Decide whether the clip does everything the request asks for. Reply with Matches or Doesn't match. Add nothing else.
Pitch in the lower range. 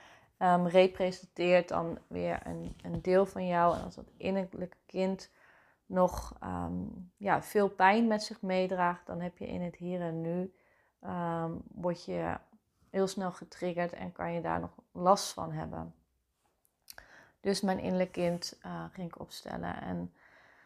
Doesn't match